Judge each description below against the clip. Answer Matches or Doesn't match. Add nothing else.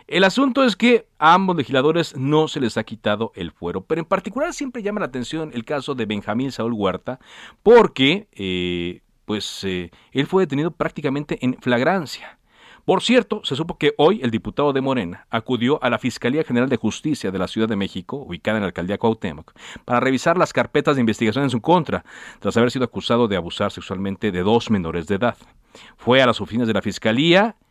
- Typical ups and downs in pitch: Doesn't match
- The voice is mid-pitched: Doesn't match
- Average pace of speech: Doesn't match